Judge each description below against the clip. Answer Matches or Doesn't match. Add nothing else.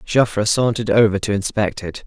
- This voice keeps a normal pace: Matches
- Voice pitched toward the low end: Matches